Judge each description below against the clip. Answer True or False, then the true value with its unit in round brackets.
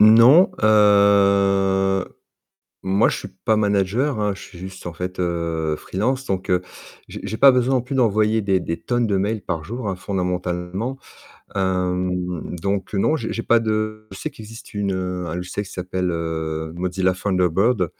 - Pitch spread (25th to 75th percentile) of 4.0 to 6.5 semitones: False (3.0 semitones)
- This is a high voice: False (95 Hz)